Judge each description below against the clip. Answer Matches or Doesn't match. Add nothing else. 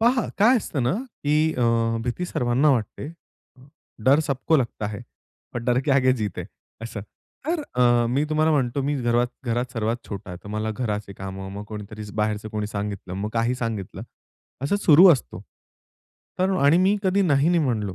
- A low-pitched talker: Matches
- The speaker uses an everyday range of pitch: Doesn't match